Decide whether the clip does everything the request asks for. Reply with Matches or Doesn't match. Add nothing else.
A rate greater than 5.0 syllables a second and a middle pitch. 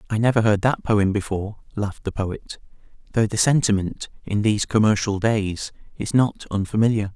Doesn't match